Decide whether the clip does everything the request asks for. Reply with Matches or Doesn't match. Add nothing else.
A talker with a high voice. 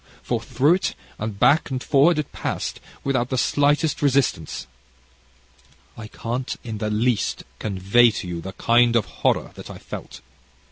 Doesn't match